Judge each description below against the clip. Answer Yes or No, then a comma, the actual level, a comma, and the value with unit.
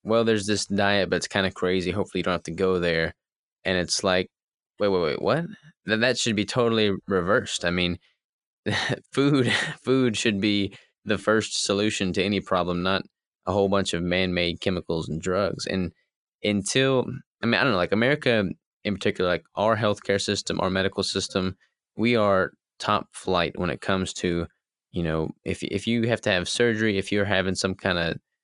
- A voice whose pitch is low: Yes, low, 100 Hz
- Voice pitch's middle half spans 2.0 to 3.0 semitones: No, average, 3.4 semitones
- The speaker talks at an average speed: Yes, average, 195 wpm